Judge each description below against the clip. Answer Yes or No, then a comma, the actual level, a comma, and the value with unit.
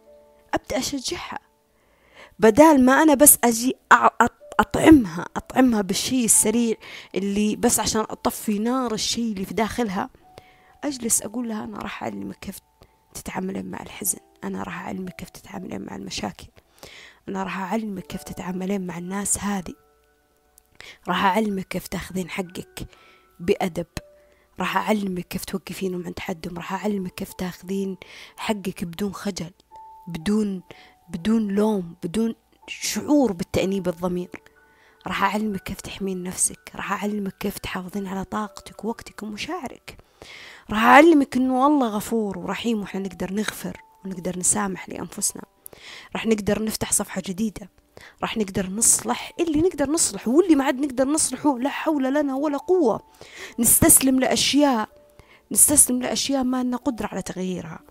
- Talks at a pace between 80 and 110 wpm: No, average, 130 wpm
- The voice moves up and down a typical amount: Yes, average, 4.7 semitones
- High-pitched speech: Yes, high, 205 Hz